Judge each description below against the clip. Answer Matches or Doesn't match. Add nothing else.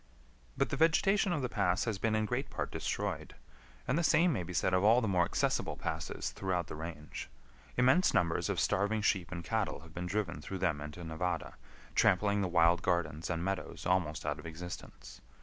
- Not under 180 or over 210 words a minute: Matches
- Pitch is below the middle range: Matches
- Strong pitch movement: Doesn't match